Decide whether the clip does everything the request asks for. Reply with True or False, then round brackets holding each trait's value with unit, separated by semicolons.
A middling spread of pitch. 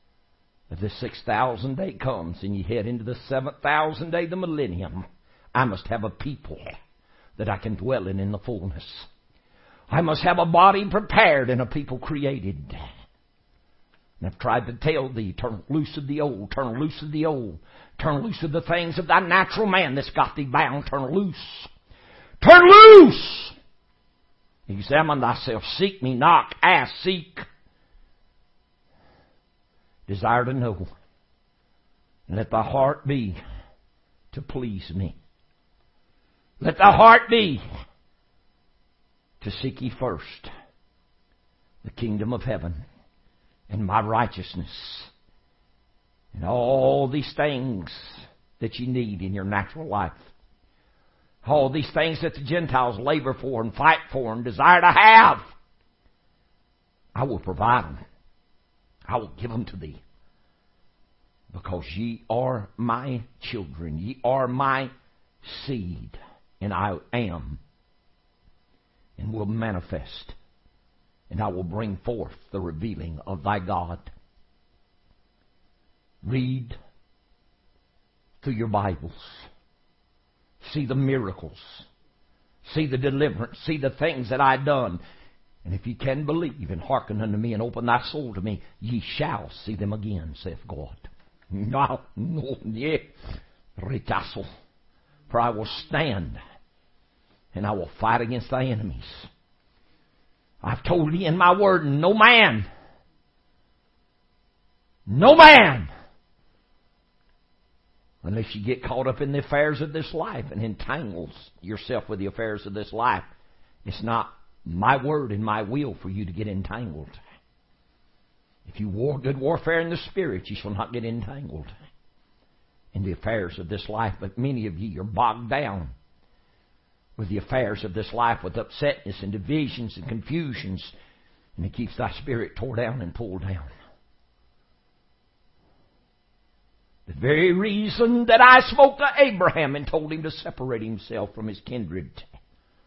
False (6.3 semitones)